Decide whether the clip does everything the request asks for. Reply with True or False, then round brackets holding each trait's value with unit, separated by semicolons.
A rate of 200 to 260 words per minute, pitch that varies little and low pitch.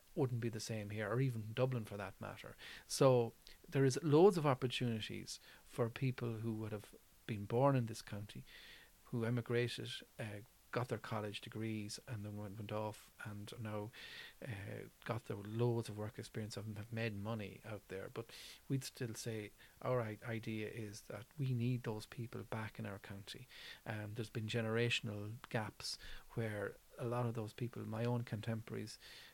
False (170 wpm; 2.2 semitones; 115 Hz)